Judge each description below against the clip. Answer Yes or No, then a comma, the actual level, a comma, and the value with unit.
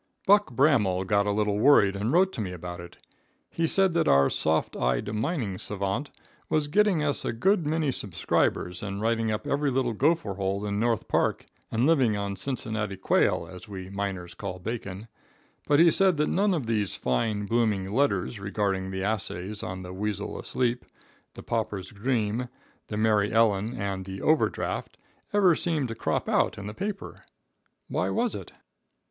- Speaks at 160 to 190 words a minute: Yes, average, 175 wpm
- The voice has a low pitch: Yes, low, 105 Hz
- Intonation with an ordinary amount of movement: No, wide, 6.3 semitones